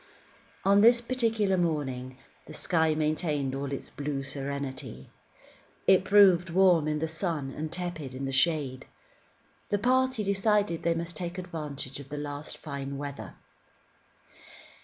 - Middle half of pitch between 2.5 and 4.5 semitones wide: No, average, 5.0 semitones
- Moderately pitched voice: Yes, medium, 155 Hz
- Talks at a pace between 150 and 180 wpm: No, average, 140 wpm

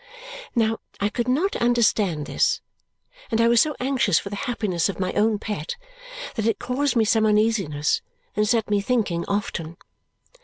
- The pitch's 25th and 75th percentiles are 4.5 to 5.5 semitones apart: No, average, 3.1 semitones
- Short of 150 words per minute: No, average, 165 wpm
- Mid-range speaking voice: No, high, 220 Hz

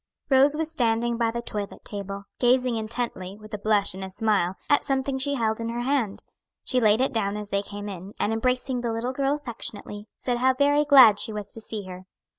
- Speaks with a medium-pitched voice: No, high, 230 Hz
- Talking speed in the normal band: No, fast, 220 wpm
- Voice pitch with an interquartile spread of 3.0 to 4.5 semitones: Yes, average, 3.8 semitones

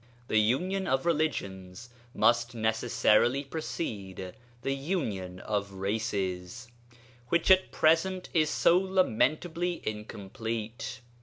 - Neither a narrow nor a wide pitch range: No, wide, 7.5 semitones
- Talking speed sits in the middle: No, slow, 95 wpm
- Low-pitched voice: Yes, low, 120 Hz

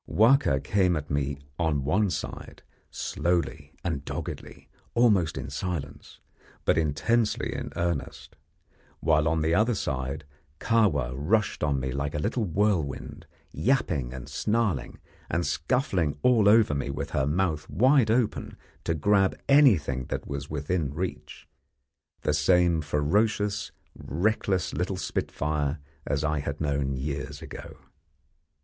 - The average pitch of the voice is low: Yes, very low, 80 Hz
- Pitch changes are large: Yes, wide, 6.1 semitones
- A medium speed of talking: No, slow, 130 wpm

